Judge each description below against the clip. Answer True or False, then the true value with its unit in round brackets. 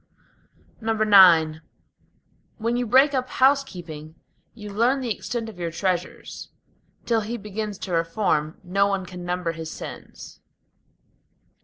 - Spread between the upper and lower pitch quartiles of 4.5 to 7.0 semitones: True (4.9 semitones)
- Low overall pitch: False (200 Hz)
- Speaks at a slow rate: True (125 wpm)